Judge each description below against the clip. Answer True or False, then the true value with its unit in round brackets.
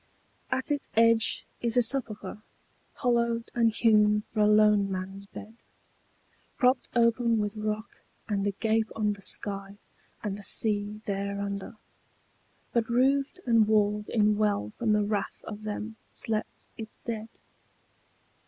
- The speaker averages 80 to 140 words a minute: True (135 wpm)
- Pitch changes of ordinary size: False (2.0 semitones)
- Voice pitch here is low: False (215 Hz)